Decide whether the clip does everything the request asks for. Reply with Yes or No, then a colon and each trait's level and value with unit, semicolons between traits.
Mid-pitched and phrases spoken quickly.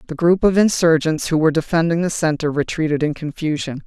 No: medium, 160 Hz; average, 185 wpm